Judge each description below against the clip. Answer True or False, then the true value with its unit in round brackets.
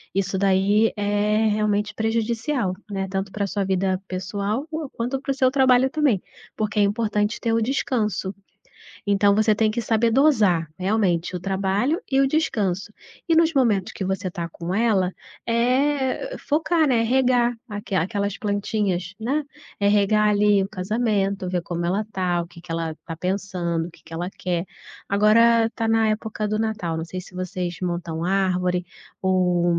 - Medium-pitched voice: False (205 Hz)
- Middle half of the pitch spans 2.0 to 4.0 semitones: True (3.6 semitones)